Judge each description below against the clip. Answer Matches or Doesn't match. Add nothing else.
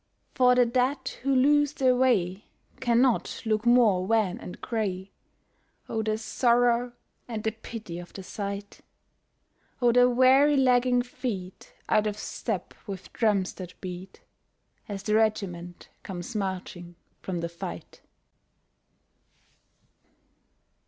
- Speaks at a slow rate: Matches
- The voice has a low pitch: Doesn't match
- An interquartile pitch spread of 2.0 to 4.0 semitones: Doesn't match